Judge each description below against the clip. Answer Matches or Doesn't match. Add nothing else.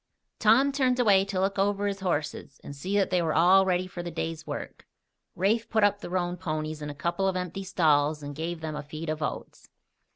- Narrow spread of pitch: Doesn't match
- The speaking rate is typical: Doesn't match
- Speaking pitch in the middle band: Matches